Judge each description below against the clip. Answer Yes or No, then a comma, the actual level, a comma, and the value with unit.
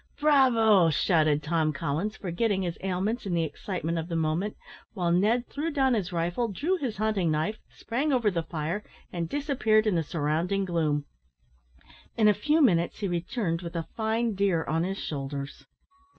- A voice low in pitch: No, medium, 185 Hz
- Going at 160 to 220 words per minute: Yes, average, 170 wpm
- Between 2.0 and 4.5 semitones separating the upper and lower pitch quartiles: No, average, 5.0 semitones